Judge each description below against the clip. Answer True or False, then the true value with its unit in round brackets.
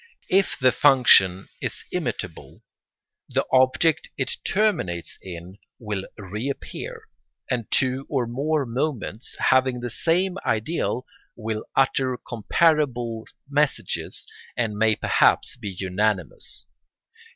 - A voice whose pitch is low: True (125 Hz)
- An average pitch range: True (4.6 semitones)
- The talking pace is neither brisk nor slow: False (105 wpm)